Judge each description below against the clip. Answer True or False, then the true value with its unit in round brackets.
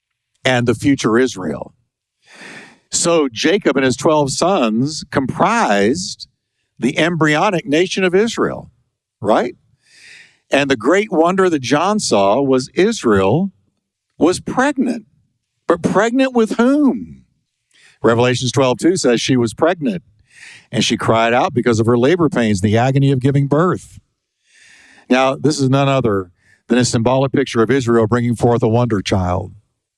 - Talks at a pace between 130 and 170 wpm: True (140 wpm)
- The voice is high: False (135 Hz)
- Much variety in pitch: True (5.8 semitones)